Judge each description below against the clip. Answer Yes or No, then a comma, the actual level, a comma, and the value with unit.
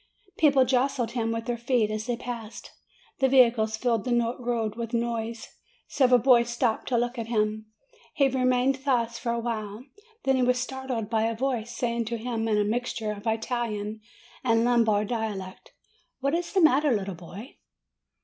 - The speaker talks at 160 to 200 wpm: Yes, average, 175 wpm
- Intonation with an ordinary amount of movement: No, narrow, 2.2 semitones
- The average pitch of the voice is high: Yes, high, 235 Hz